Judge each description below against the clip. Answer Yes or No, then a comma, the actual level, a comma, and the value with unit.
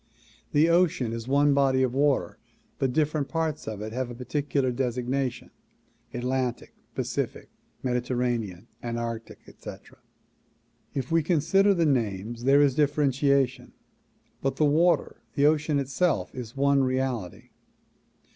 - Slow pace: Yes, slow, 120 wpm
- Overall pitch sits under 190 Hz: Yes, low, 135 Hz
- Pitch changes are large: No, average, 3.1 semitones